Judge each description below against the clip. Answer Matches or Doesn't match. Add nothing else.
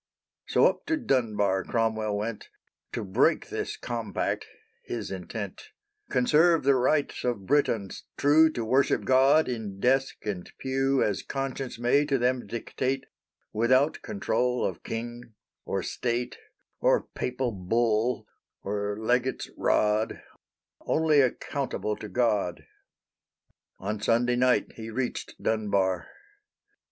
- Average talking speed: Doesn't match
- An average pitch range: Matches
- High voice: Doesn't match